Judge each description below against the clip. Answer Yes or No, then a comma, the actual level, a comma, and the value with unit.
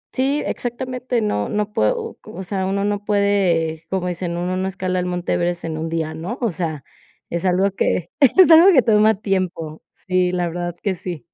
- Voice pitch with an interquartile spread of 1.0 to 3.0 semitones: No, average, 3.4 semitones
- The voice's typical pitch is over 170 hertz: Yes, medium, 185 Hz